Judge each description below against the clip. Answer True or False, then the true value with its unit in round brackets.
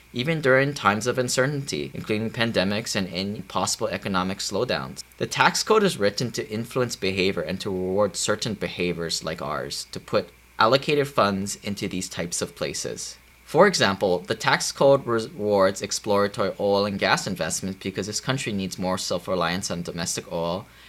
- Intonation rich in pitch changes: False (4.1 semitones)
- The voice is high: False (100 Hz)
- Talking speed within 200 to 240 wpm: False (165 wpm)